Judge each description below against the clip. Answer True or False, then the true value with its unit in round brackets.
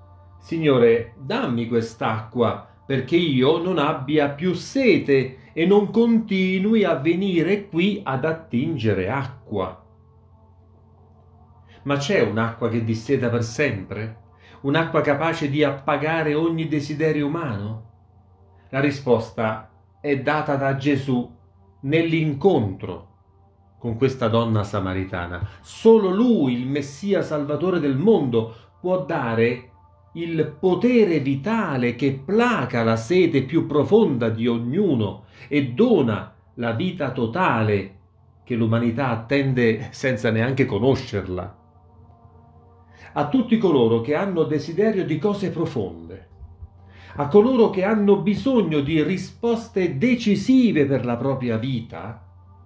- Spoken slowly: True (110 wpm)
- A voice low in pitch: True (130 Hz)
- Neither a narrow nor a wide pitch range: False (7.2 semitones)